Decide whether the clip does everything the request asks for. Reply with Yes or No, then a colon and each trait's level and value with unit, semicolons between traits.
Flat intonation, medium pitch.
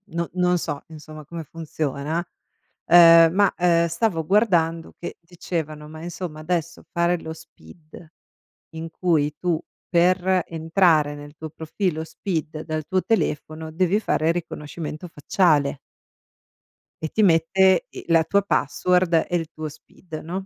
Yes: narrow, 2.2 semitones; medium, 165 Hz